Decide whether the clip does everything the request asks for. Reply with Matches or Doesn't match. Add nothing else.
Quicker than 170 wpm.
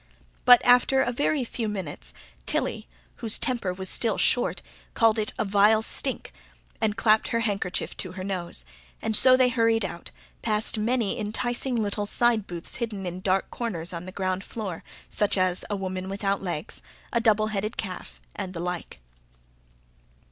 Doesn't match